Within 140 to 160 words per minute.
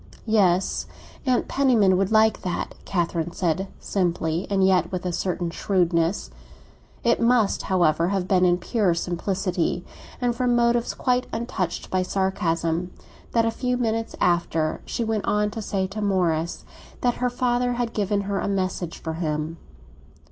Yes: average, 150 wpm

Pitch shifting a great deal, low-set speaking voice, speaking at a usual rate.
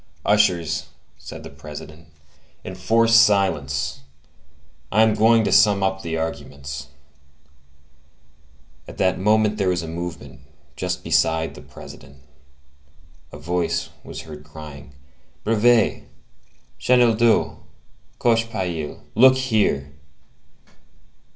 No: wide, 6.1 semitones; very low, 90 Hz; slow, 100 wpm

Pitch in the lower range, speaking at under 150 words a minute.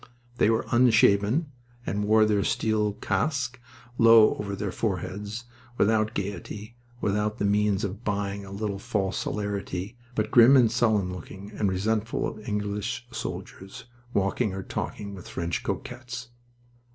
Yes: low, 105 Hz; average, 140 wpm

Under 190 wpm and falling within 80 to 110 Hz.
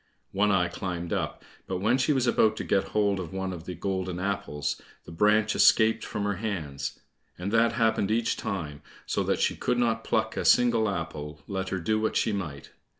No: fast, 205 wpm; low, 100 Hz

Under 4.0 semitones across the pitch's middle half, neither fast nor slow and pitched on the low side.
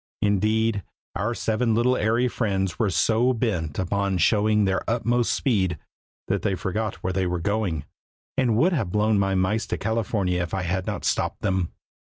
Yes: average, 3.2 semitones; average, 175 wpm; low, 105 Hz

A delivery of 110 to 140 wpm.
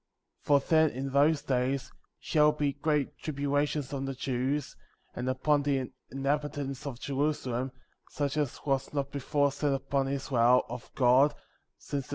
No: average, 155 wpm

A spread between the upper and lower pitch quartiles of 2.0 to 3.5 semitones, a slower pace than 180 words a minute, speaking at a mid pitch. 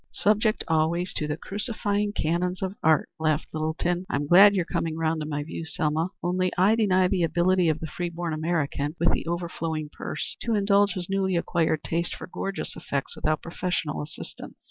No: average, 3.0 semitones; average, 185 wpm; medium, 170 Hz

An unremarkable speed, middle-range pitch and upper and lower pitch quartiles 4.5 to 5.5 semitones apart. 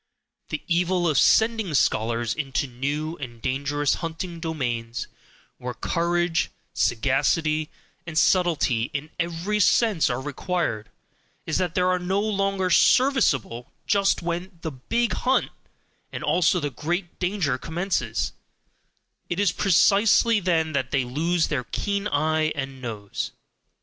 No: slow, 130 wpm; medium, 160 Hz; average, 5.1 semitones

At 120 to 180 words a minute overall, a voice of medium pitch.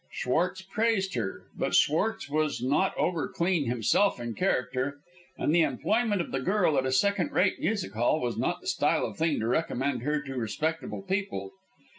Yes: average, 175 wpm; medium, 155 Hz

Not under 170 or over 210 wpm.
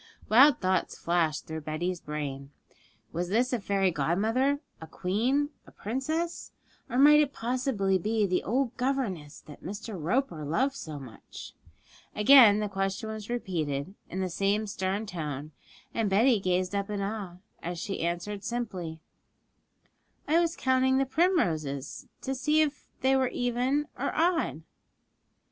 No: average, 145 wpm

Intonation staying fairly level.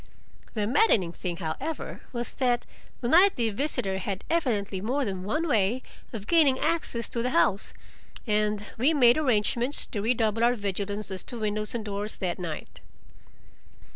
No: average, 4.0 semitones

